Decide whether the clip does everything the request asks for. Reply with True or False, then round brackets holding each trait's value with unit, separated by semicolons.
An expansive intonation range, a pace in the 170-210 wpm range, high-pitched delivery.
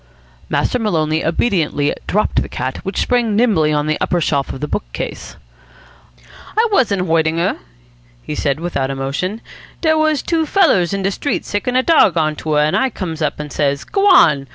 False (8.0 semitones; 190 wpm; 175 Hz)